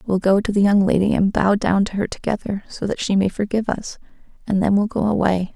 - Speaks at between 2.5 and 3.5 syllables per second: No, 6.0 syllables/s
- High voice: Yes, high, 200 Hz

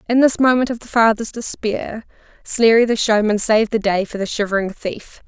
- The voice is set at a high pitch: Yes, high, 220 Hz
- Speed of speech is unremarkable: Yes, average, 195 wpm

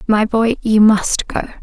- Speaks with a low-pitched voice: No, high, 220 Hz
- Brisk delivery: No, average, 185 wpm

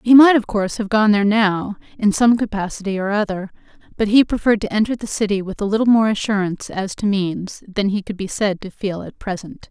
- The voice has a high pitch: Yes, high, 205 Hz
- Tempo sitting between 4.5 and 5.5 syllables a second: No, 5.9 syllables/s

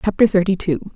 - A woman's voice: Yes, female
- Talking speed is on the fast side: No, average, 190 wpm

